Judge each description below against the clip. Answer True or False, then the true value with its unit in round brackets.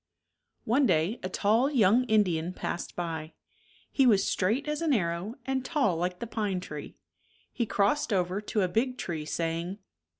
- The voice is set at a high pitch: True (200 Hz)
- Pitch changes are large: True (5.8 semitones)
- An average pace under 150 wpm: False (165 wpm)